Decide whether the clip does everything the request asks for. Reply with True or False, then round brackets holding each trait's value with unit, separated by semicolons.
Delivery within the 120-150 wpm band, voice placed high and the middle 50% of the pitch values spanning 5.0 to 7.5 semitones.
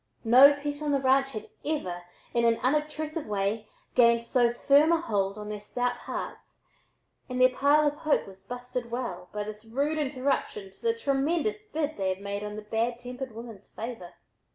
False (185 wpm; 245 Hz; 5.3 semitones)